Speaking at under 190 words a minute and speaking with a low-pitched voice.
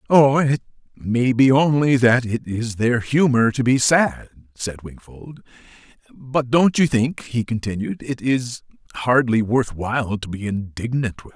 Yes: average, 165 wpm; low, 125 Hz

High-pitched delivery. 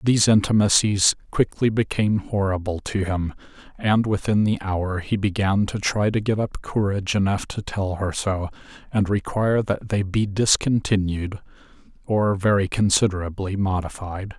No: low, 100 Hz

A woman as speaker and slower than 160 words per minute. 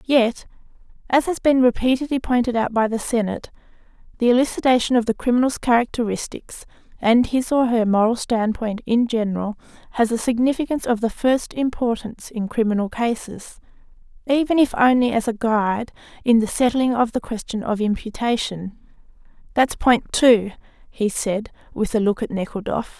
Yes: female; average, 150 wpm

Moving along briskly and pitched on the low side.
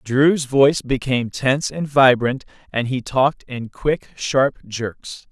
No: average, 145 wpm; low, 130 Hz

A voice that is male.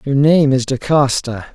Yes: male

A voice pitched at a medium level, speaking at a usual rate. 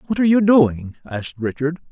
Yes: medium, 155 Hz; average, 190 wpm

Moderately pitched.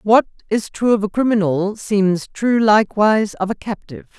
No: high, 205 Hz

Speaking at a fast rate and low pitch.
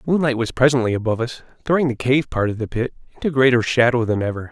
Yes: fast, 225 wpm; low, 125 Hz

